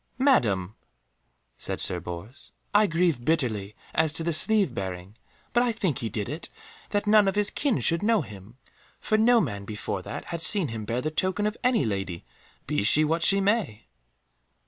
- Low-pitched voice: No, medium, 160 Hz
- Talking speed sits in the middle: Yes, average, 185 wpm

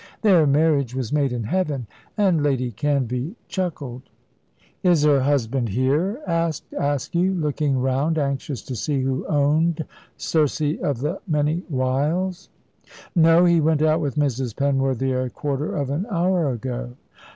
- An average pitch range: Yes, average, 3.7 semitones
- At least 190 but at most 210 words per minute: No, average, 140 wpm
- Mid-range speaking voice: Yes, medium, 145 Hz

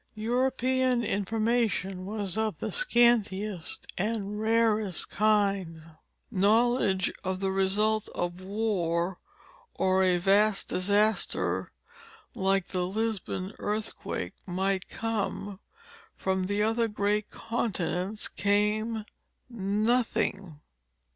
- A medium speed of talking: No, slow, 95 wpm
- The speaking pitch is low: No, high, 205 Hz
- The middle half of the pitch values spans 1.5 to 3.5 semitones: Yes, average, 2.7 semitones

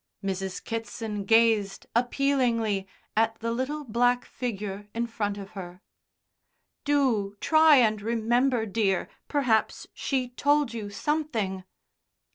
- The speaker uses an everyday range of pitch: Yes, average, 3.7 semitones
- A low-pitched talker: No, high, 225 Hz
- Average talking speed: No, slow, 110 wpm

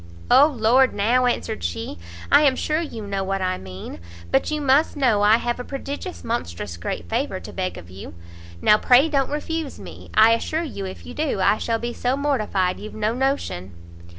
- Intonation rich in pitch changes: Yes, wide, 6.1 semitones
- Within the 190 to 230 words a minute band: Yes, average, 200 wpm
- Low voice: No, high, 235 Hz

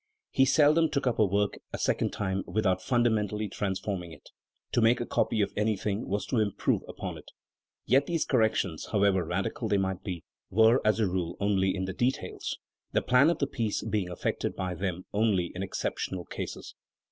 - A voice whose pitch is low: Yes, low, 105 Hz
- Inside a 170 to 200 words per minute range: Yes, average, 190 wpm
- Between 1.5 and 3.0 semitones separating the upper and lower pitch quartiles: No, average, 3.7 semitones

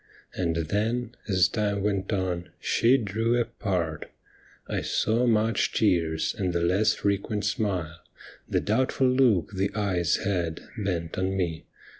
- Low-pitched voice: Yes, low, 100 Hz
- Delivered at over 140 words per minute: No, slow, 135 wpm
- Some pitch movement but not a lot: Yes, average, 3.8 semitones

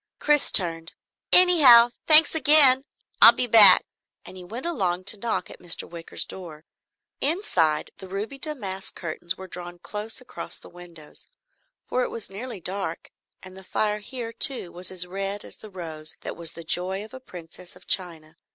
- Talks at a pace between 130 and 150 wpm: No, average, 175 wpm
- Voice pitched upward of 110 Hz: Yes, high, 190 Hz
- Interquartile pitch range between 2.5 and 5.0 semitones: No, wide, 5.6 semitones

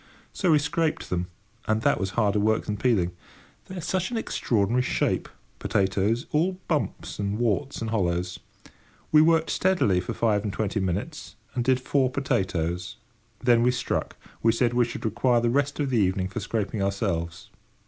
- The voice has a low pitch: Yes, low, 115 Hz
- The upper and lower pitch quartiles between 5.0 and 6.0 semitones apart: Yes, average, 5.3 semitones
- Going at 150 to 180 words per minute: Yes, average, 170 wpm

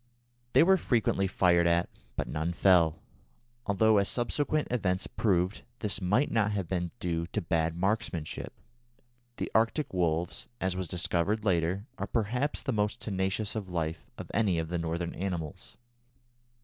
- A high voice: No, very low, 95 Hz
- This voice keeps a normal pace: Yes, average, 150 wpm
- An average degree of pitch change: Yes, average, 3.9 semitones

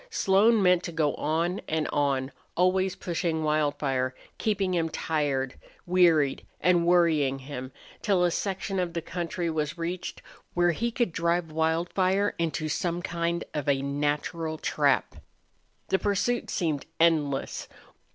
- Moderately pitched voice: Yes, medium, 170 Hz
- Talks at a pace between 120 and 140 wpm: Yes, slow, 135 wpm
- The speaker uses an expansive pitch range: No, average, 3.3 semitones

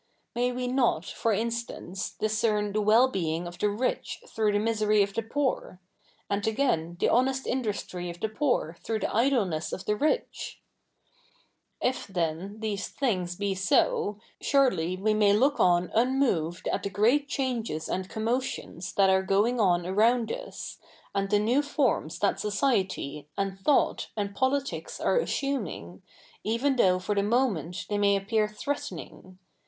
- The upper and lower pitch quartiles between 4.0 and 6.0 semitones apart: Yes, average, 4.6 semitones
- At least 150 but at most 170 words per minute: Yes, average, 160 wpm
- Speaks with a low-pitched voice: No, high, 210 Hz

